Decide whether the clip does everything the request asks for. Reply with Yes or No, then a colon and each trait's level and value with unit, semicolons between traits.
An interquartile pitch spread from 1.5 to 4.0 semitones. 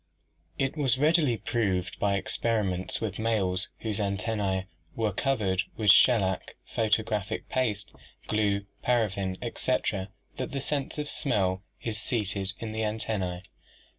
Yes: average, 3.3 semitones